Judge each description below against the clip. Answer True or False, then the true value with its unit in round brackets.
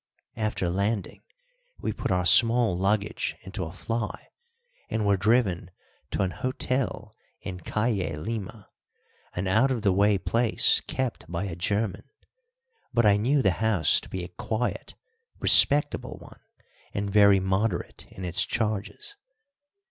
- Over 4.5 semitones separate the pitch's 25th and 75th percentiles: False (3.3 semitones)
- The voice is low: True (100 Hz)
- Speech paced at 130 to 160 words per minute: True (140 wpm)